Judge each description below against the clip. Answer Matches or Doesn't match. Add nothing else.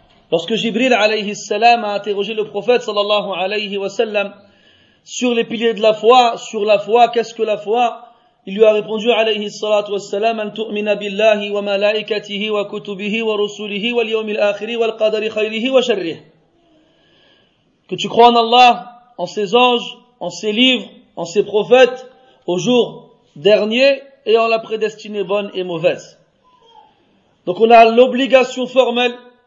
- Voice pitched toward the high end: Matches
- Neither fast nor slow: Doesn't match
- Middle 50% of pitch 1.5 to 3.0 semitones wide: Matches